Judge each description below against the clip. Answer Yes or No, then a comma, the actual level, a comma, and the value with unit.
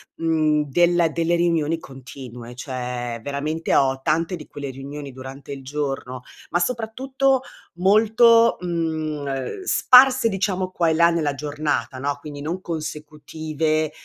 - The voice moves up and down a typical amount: Yes, average, 4.1 semitones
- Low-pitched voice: No, medium, 155 Hz